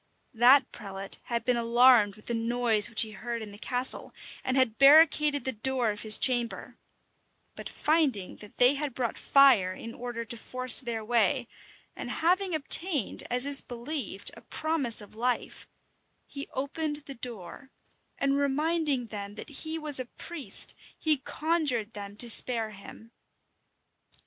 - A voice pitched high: Yes, high, 245 Hz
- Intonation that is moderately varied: Yes, average, 4.0 semitones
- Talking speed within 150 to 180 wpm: Yes, average, 155 wpm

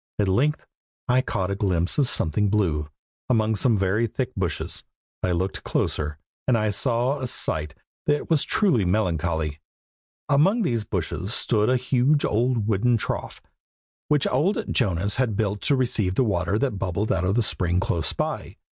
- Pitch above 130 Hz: No, low, 105 Hz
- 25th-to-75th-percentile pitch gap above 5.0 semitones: Yes, wide, 5.6 semitones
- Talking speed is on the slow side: No, average, 165 wpm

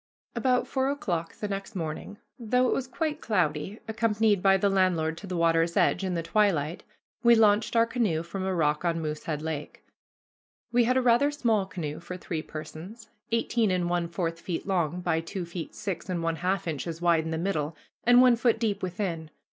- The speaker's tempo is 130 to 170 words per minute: No, average, 195 wpm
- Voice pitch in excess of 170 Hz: Yes, medium, 185 Hz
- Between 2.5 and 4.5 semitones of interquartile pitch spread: No, average, 5.1 semitones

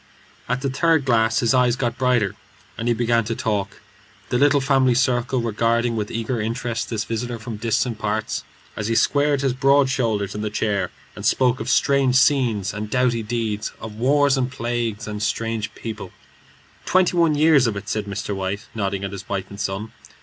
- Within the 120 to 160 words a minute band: No, average, 190 wpm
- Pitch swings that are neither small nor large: Yes, average, 3.3 semitones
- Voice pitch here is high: No, low, 115 Hz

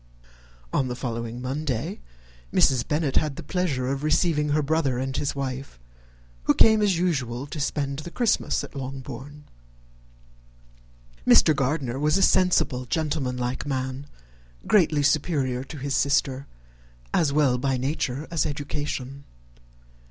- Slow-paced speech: Yes, slow, 130 wpm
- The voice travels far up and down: No, average, 2.9 semitones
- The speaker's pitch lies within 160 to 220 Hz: No, medium, 140 Hz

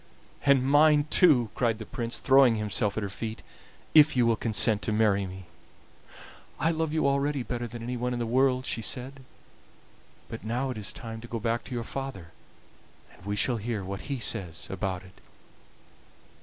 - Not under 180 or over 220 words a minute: Yes, average, 185 wpm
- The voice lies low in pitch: Yes, low, 120 Hz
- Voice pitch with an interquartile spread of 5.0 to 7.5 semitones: No, average, 3.8 semitones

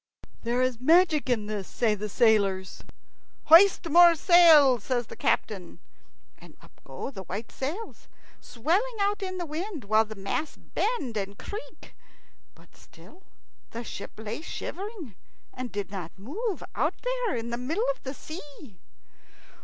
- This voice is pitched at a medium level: No, very high, 265 Hz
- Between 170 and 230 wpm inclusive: No, average, 150 wpm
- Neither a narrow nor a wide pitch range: No, wide, 8.4 semitones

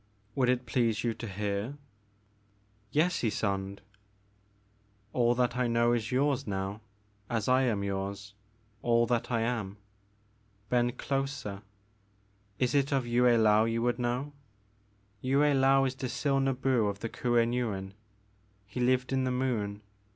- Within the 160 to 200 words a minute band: No, average, 145 wpm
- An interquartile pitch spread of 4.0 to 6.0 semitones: No, average, 3.6 semitones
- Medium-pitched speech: No, low, 120 Hz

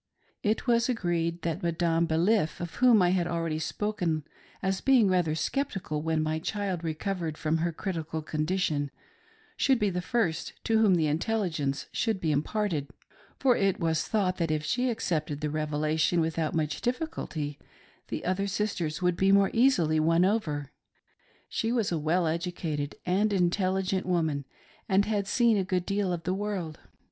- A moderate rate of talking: Yes, average, 165 wpm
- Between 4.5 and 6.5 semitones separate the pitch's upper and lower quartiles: No, average, 4.1 semitones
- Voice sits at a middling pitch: Yes, medium, 175 Hz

